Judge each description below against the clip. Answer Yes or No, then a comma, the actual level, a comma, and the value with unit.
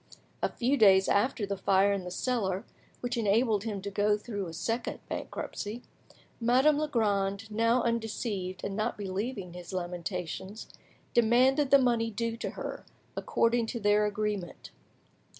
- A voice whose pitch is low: No, high, 210 Hz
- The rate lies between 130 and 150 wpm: Yes, average, 145 wpm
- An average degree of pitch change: Yes, average, 3.3 semitones